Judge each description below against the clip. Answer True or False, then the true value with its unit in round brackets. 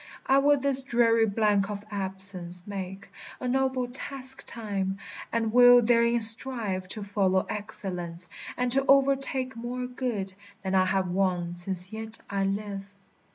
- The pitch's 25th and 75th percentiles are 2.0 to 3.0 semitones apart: False (4.5 semitones)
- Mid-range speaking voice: False (215 Hz)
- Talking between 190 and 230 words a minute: False (145 wpm)